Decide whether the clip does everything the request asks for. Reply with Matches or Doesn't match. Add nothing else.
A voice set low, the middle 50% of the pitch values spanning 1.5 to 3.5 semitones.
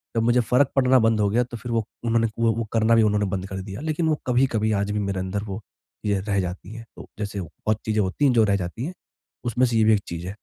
Matches